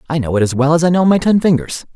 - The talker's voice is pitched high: No, medium, 155 Hz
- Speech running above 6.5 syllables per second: Yes, 7.0 syllables/s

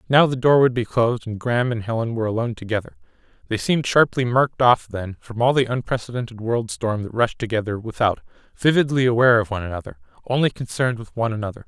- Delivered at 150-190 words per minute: No, average, 200 wpm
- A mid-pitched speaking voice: No, low, 115 Hz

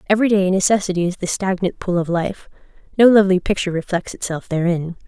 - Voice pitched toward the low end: No, medium, 185 Hz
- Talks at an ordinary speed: Yes, average, 155 wpm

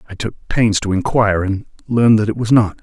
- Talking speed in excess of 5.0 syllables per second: Yes, 5.8 syllables/s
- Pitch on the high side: No, low, 105 Hz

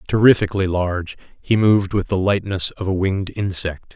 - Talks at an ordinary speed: Yes, average, 165 wpm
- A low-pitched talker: Yes, very low, 95 Hz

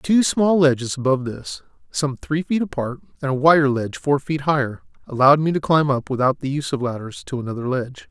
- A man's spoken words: Yes, male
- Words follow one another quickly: Yes, fast, 215 wpm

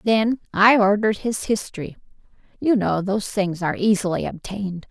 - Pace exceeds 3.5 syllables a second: Yes, 5.5 syllables/s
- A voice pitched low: No, high, 200 Hz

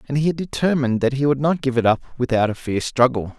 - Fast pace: Yes, fast, 265 wpm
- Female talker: No, male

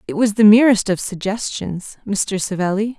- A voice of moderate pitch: No, high, 205 Hz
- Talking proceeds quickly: No, average, 160 wpm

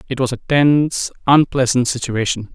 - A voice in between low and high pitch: No, low, 130 Hz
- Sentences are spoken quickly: No, average, 140 wpm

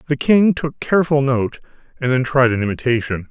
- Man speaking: Yes, male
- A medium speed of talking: Yes, average, 180 wpm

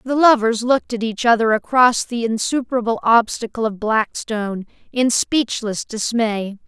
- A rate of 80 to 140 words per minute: Yes, slow, 135 wpm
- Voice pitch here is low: No, high, 230 Hz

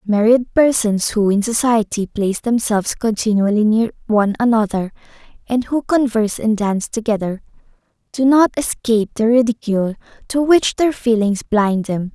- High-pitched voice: Yes, high, 225 Hz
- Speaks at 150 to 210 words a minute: No, average, 140 wpm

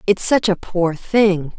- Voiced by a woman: Yes, female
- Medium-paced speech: Yes, average, 190 wpm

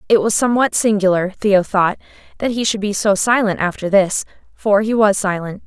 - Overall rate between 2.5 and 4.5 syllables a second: No, 5.3 syllables/s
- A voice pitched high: Yes, high, 205 Hz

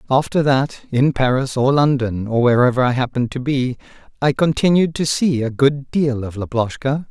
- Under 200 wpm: Yes, average, 175 wpm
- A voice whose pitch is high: No, low, 135 Hz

